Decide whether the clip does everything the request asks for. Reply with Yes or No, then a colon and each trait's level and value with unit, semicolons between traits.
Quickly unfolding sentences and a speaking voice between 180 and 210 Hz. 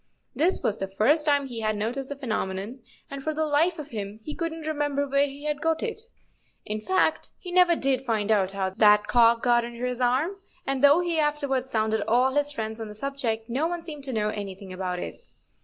No: fast, 225 wpm; very high, 265 Hz